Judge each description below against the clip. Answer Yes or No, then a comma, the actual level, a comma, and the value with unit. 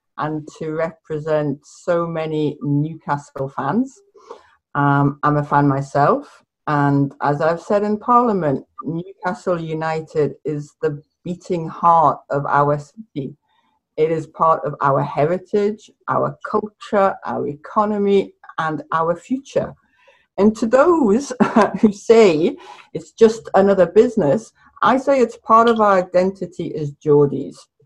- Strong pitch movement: Yes, wide, 6.2 semitones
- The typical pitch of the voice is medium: Yes, medium, 170 Hz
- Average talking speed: No, slow, 125 wpm